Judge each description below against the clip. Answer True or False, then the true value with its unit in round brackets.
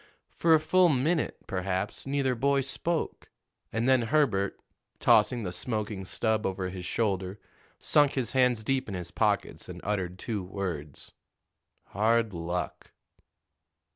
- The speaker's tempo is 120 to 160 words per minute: True (135 wpm)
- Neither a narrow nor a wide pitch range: False (5.9 semitones)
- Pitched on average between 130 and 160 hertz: False (110 Hz)